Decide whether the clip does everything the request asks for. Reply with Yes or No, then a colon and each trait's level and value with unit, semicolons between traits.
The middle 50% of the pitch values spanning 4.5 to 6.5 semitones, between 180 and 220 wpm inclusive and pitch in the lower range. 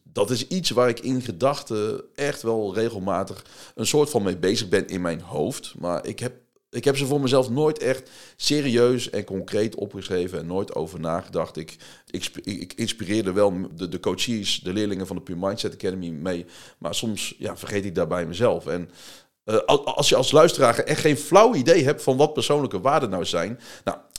Yes: average, 5.1 semitones; average, 195 wpm; low, 110 Hz